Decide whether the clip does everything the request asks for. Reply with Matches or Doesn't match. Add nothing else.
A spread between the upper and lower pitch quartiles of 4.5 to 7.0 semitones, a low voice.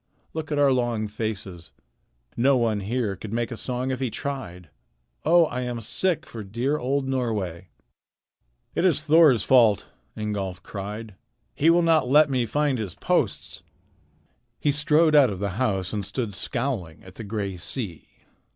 Matches